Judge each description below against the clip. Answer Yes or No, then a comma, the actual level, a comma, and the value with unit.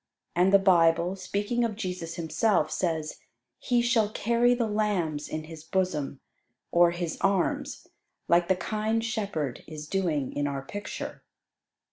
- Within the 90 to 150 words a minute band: Yes, average, 140 wpm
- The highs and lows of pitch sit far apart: No, average, 4.7 semitones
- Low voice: No, medium, 180 Hz